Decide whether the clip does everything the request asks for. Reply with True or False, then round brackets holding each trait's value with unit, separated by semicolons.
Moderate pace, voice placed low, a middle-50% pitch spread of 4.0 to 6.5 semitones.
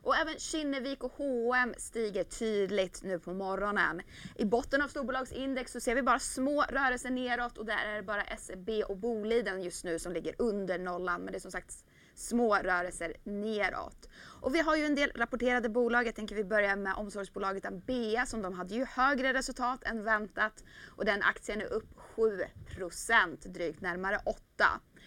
False (180 wpm; 230 Hz; 4.4 semitones)